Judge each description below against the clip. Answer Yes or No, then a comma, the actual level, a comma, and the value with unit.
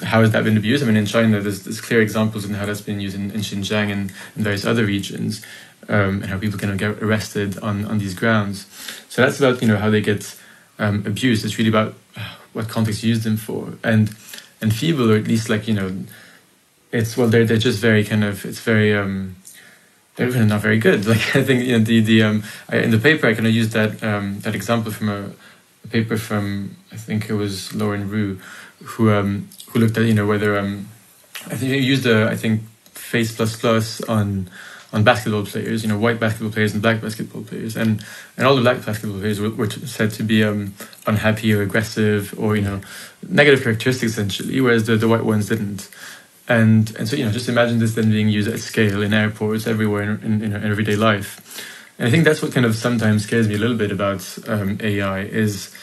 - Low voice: Yes, low, 110 Hz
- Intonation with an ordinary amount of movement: No, narrow, 1.6 semitones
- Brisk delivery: Yes, fast, 230 wpm